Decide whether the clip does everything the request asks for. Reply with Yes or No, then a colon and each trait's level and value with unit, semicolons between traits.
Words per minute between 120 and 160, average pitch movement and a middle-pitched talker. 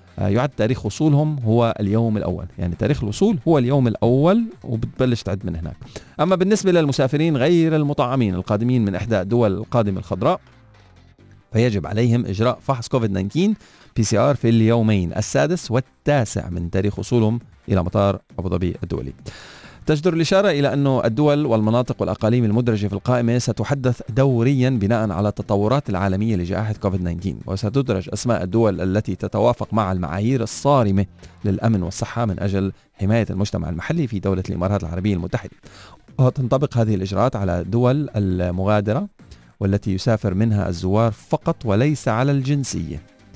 No: fast, 135 wpm; average, 4.7 semitones; low, 110 Hz